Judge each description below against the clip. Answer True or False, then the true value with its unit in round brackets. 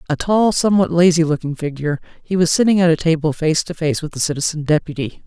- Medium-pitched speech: True (160 Hz)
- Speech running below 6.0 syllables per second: False (6.4 syllables/s)